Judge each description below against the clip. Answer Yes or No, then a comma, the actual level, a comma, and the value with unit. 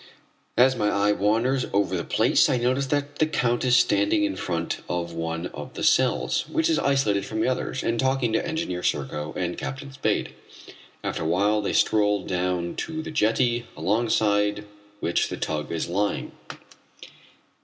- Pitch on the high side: No, low, 110 Hz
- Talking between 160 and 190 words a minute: Yes, average, 170 wpm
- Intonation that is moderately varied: No, wide, 6.3 semitones